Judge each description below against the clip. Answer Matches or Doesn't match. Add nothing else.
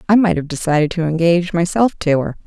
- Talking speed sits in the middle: Doesn't match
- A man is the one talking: Doesn't match